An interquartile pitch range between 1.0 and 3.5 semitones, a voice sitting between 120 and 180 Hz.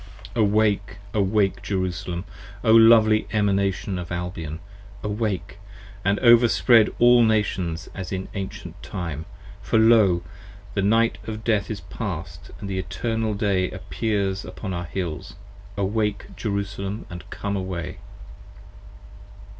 No: average, 3.0 semitones; low, 100 Hz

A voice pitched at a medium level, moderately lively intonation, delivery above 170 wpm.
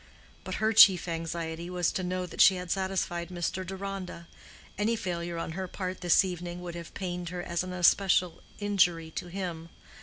No: medium, 180 Hz; narrow, 1.7 semitones; average, 180 wpm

